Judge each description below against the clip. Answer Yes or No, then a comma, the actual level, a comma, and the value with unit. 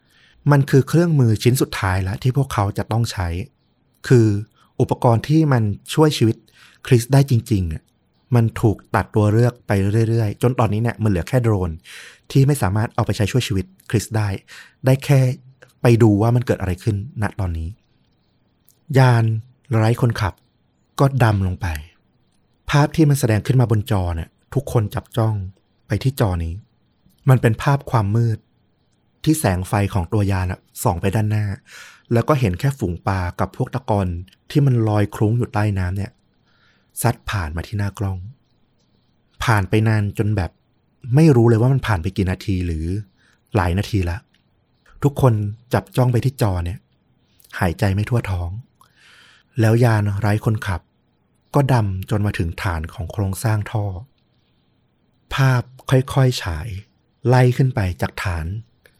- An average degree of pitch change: Yes, average, 3.9 semitones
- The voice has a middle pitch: No, low, 110 Hz